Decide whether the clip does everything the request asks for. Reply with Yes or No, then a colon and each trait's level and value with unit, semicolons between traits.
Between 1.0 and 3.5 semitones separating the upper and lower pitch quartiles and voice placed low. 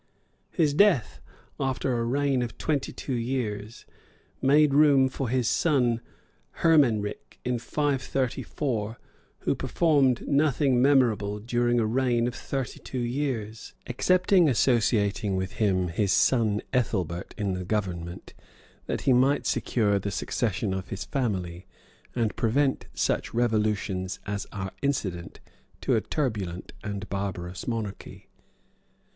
No: average, 4.7 semitones; low, 120 Hz